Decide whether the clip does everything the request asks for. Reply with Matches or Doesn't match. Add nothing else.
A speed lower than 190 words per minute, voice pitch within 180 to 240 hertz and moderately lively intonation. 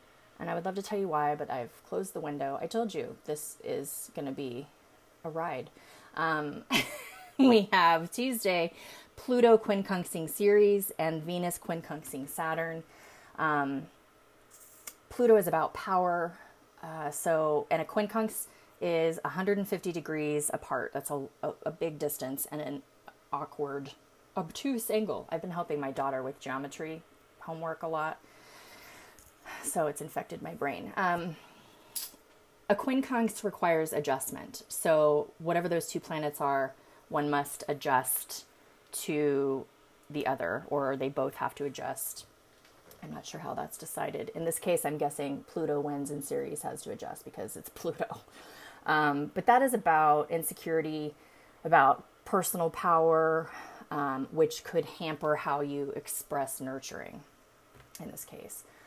Doesn't match